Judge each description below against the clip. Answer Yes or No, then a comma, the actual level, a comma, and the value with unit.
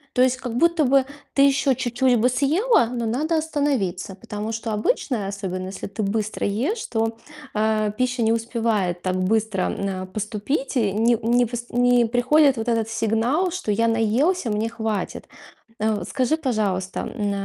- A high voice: Yes, high, 230 Hz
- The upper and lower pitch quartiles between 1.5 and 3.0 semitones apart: No, average, 3.5 semitones